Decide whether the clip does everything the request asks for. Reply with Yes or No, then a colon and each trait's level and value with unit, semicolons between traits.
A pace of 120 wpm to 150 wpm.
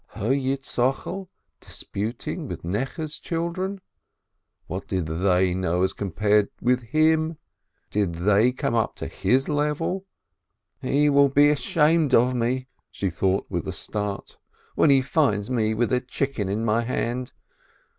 Yes: average, 145 wpm